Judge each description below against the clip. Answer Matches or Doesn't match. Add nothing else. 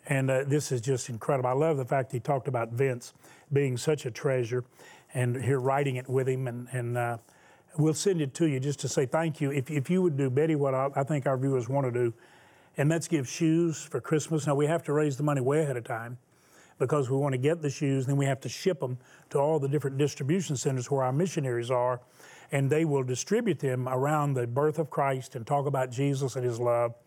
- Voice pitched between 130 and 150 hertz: Matches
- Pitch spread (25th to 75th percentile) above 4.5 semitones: Doesn't match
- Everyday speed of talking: Doesn't match